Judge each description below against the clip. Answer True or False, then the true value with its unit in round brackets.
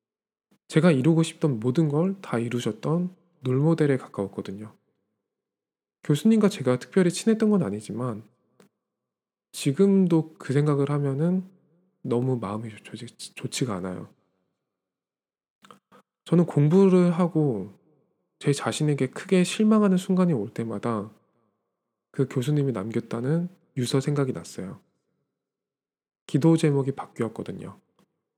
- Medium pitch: True (145 Hz)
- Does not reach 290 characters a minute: True (250 characters per minute)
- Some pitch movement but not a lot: False (6.7 semitones)